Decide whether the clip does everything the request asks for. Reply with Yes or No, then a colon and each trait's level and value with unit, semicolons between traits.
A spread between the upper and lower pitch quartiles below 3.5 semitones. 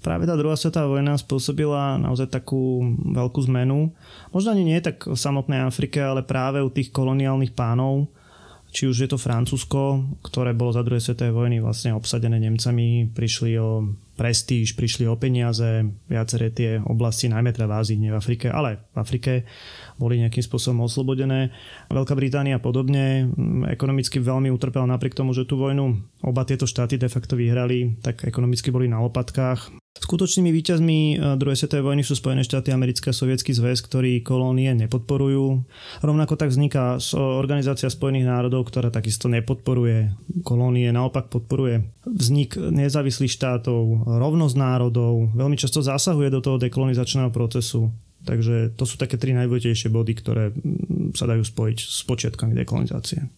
Yes: narrow, 2.4 semitones